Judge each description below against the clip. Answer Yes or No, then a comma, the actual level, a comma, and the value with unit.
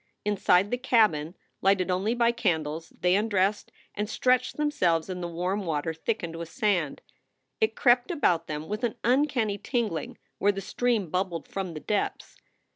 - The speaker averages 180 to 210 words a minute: No, average, 165 wpm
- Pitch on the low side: No, high, 195 Hz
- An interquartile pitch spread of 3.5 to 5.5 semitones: Yes, average, 5.2 semitones